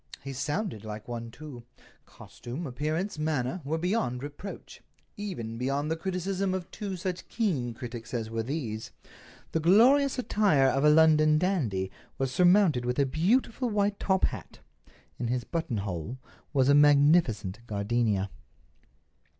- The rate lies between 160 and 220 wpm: No, slow, 135 wpm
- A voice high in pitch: No, medium, 145 Hz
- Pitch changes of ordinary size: No, wide, 7.1 semitones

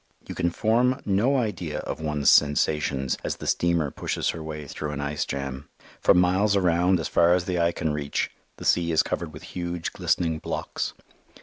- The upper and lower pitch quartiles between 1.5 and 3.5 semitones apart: Yes, average, 3.2 semitones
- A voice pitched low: Yes, very low, 85 Hz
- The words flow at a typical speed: Yes, average, 190 wpm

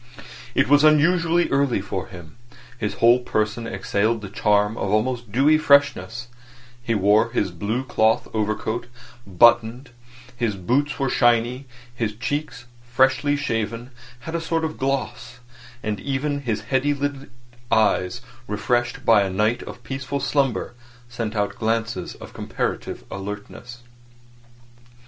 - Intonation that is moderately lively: Yes, average, 4.1 semitones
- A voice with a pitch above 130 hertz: No, low, 120 Hz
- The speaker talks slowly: Yes, slow, 130 wpm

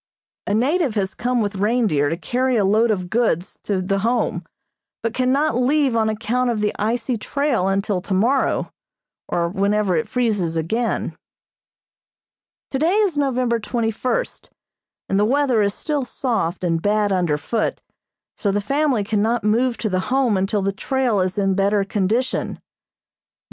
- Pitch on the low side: No, high, 220 Hz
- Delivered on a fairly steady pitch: No, average, 4.2 semitones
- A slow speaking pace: No, average, 155 wpm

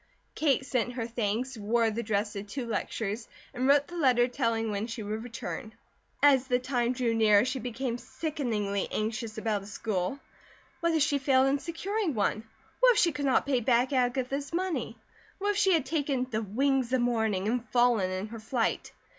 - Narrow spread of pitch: No, average, 3.7 semitones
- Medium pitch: No, high, 245 Hz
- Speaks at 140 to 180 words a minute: No, average, 190 wpm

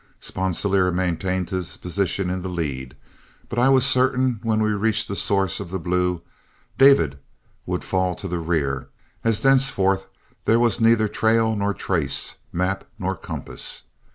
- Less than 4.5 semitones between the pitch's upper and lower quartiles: Yes, average, 3.9 semitones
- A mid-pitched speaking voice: No, very low, 95 Hz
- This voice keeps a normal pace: Yes, average, 155 wpm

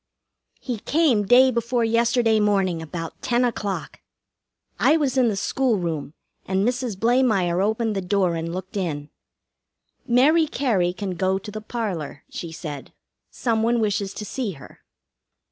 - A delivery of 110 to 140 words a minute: No, average, 150 wpm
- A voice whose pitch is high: Yes, high, 210 Hz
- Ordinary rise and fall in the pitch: Yes, average, 4.7 semitones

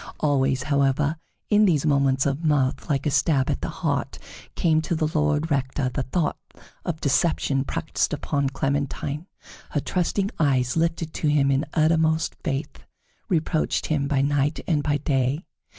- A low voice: No, medium, 145 Hz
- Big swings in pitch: No, narrow, 2.5 semitones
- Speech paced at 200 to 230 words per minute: No, average, 155 wpm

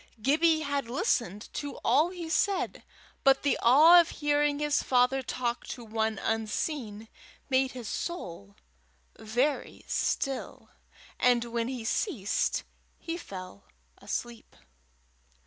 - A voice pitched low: No, very high, 255 Hz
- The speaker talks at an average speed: No, slow, 115 wpm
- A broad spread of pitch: No, average, 4.8 semitones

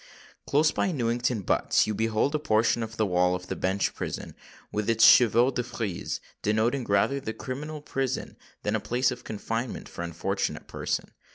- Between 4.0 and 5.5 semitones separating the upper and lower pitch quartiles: No, average, 3.6 semitones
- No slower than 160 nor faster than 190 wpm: Yes, average, 175 wpm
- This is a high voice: No, low, 115 Hz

